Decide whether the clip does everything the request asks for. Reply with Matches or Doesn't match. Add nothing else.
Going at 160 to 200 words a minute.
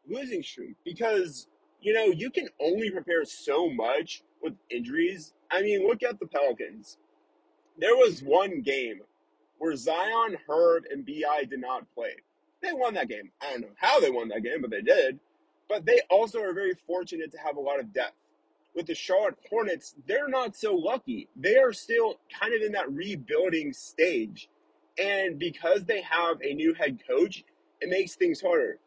Matches